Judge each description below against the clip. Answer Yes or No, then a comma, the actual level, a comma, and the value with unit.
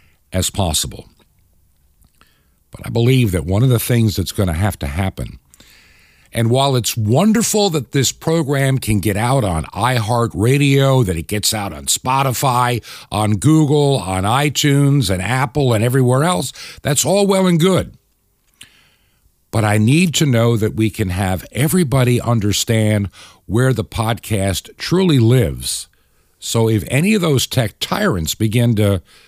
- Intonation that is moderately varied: No, wide, 5.8 semitones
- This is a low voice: Yes, low, 115 Hz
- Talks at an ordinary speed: Yes, average, 150 wpm